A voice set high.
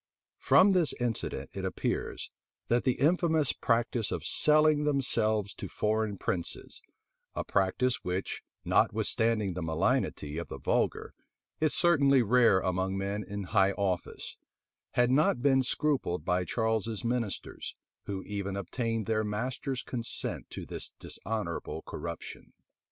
No: low, 110 Hz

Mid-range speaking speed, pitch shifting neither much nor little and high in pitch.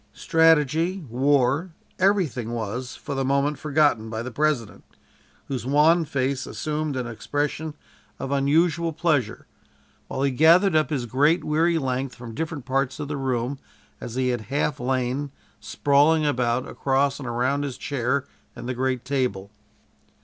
No: average, 150 wpm; average, 3.3 semitones; medium, 140 Hz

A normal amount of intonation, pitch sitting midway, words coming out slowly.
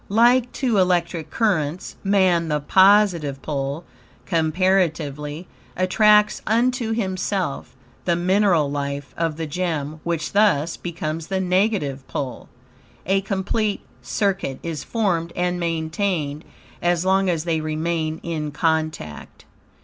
Yes: average, 3.9 semitones; medium, 170 Hz; slow, 115 wpm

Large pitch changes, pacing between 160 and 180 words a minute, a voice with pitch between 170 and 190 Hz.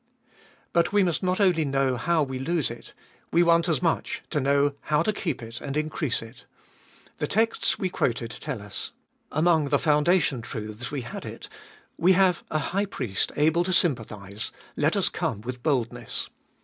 No: wide, 5.9 semitones; average, 175 wpm; medium, 150 Hz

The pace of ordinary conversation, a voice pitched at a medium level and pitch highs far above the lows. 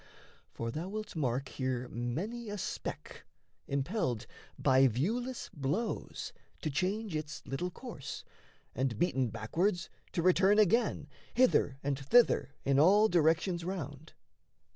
No: slow, 120 wpm; medium, 160 Hz; wide, 7.2 semitones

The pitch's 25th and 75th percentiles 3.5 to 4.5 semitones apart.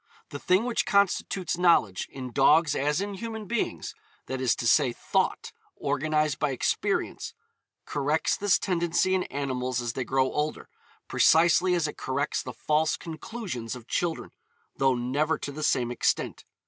No: average, 5.0 semitones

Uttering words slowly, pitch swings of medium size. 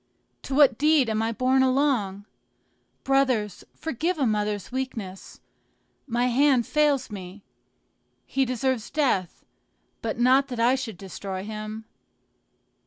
Yes: slow, 120 wpm; average, 4.2 semitones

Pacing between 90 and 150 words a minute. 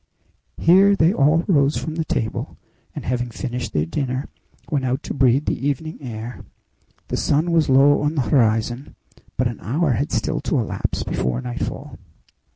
No: average, 165 wpm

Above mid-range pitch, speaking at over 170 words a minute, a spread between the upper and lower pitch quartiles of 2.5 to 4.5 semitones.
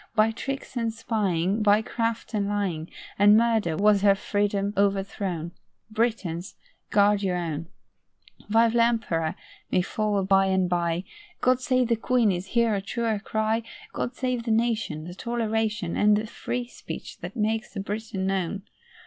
No: high, 210 Hz; average, 155 wpm; average, 2.9 semitones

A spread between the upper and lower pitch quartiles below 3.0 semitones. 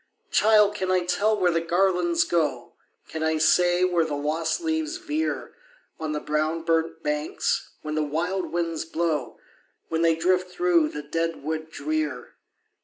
Yes: narrow, 2.5 semitones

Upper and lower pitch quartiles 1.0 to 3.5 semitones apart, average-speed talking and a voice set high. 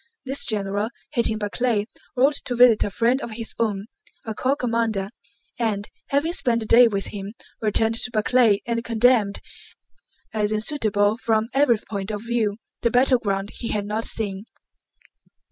Yes: average, 2.7 semitones; average, 155 wpm; high, 225 Hz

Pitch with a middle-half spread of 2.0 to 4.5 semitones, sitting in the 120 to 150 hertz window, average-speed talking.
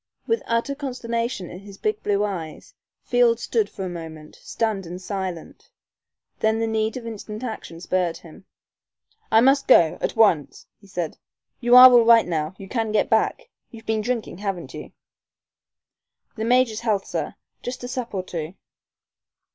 No: average, 4.2 semitones; high, 220 Hz; average, 165 wpm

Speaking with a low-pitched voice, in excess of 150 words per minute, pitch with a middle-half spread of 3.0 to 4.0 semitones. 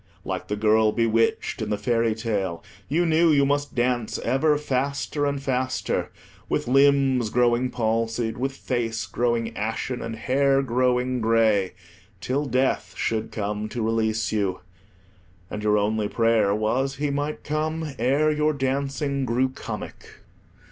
No: low, 125 Hz; average, 140 wpm; average, 3.7 semitones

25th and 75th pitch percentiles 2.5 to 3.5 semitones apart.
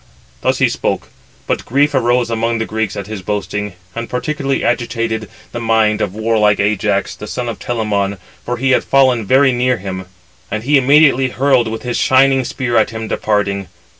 Yes: average, 3.2 semitones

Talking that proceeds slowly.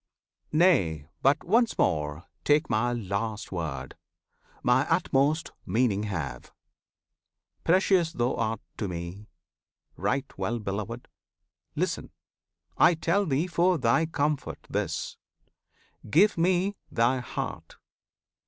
Yes: slow, 105 wpm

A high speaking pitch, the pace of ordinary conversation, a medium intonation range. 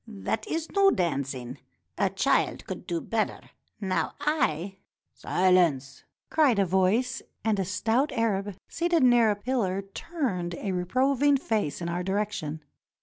No: high, 200 Hz; average, 150 wpm; wide, 5.9 semitones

